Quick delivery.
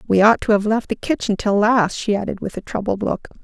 Yes: fast, 260 wpm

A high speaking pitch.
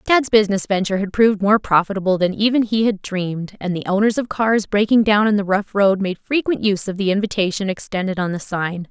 Yes: high, 200 Hz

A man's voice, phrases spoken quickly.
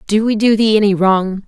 No: female; fast, 245 wpm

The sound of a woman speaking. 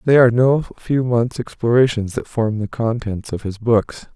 No: male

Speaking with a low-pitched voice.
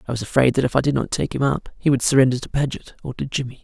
Yes: low, 130 Hz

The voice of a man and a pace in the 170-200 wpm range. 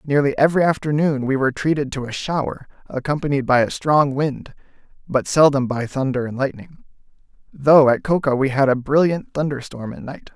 Yes: male; average, 180 wpm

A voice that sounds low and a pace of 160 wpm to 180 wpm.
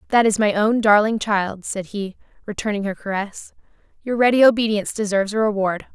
No: high, 210 Hz; average, 170 wpm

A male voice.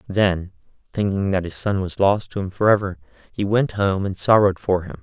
Yes: male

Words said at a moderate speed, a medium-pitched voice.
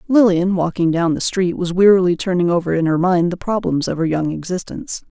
No: fast, 210 wpm; medium, 180 Hz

